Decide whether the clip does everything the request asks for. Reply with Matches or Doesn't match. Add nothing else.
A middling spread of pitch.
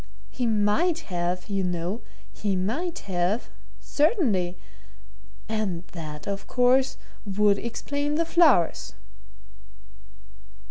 Doesn't match